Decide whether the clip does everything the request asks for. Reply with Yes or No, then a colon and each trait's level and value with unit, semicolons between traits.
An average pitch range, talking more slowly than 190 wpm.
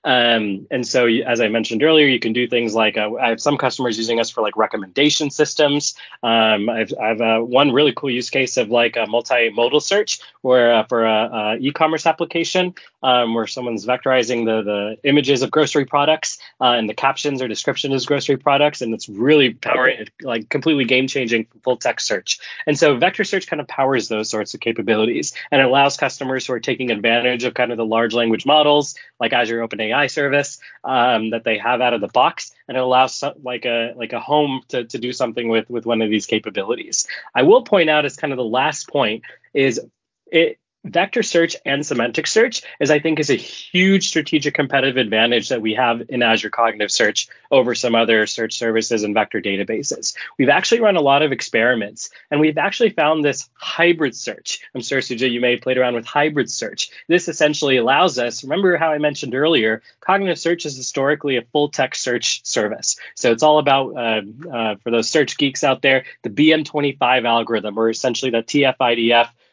No: average, 4.3 semitones; average, 200 wpm